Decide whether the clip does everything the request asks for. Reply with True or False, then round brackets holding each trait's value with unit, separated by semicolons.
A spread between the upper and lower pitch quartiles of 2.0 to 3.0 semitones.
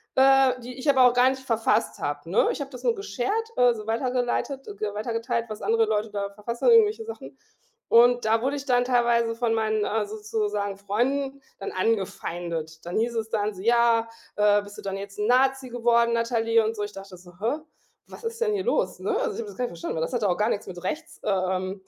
False (3.8 semitones)